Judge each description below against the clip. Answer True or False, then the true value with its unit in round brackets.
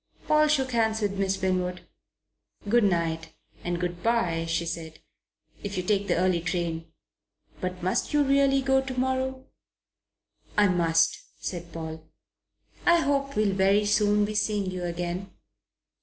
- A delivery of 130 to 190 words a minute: True (145 wpm)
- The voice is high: True (195 Hz)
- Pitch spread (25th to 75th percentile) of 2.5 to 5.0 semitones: False (5.4 semitones)